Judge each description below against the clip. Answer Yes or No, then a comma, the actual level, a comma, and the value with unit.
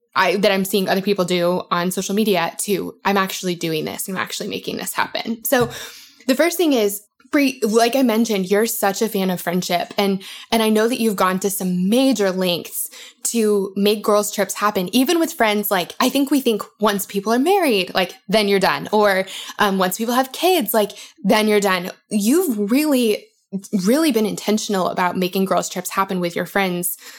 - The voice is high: Yes, high, 210 Hz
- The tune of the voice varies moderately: Yes, average, 3.3 semitones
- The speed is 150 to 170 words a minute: No, average, 195 wpm